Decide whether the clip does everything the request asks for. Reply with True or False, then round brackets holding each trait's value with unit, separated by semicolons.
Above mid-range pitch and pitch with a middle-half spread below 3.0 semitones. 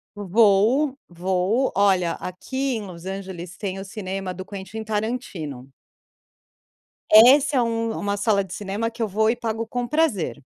False (205 Hz; 3.4 semitones)